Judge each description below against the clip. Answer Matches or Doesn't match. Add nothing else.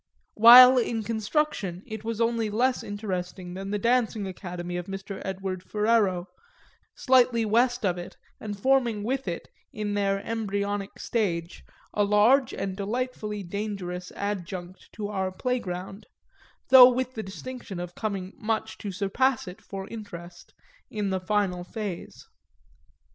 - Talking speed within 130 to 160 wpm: Matches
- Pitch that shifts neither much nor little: Matches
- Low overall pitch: Doesn't match